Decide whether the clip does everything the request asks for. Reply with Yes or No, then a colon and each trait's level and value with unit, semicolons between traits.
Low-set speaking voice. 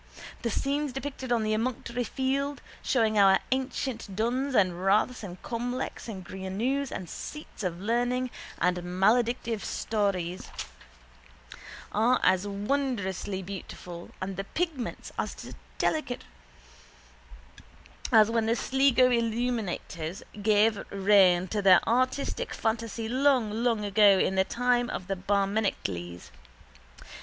No: high, 220 Hz